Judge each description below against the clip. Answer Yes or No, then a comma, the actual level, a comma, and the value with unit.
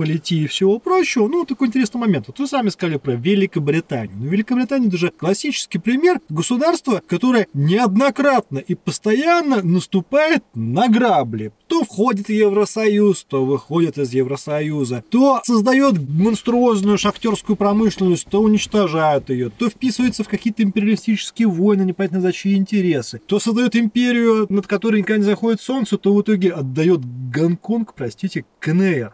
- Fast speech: No, average, 145 wpm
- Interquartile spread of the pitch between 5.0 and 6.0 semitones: Yes, wide, 5.5 semitones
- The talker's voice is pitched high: Yes, high, 205 Hz